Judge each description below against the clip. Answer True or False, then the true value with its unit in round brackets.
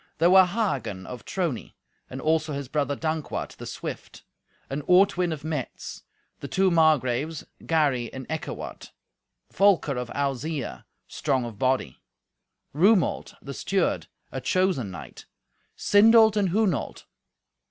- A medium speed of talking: False (125 wpm)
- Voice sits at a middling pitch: True (155 Hz)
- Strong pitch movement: True (5.7 semitones)